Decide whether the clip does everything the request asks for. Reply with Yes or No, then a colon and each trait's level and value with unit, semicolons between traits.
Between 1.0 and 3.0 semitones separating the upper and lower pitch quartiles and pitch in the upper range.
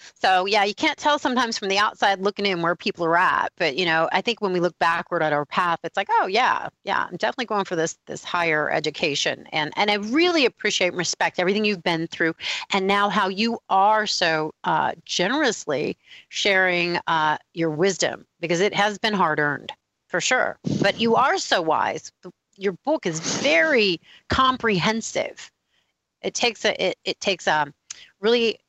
No: average, 4.3 semitones; high, 195 Hz